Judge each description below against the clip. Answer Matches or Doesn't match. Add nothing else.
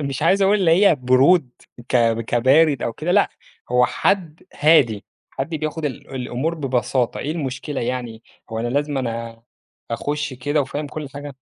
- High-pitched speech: Doesn't match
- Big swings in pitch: Doesn't match